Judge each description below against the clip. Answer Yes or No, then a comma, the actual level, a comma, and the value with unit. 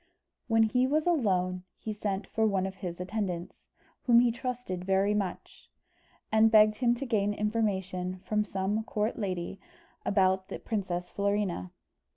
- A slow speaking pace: No, average, 150 wpm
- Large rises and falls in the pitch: No, average, 2.9 semitones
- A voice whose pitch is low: No, high, 205 Hz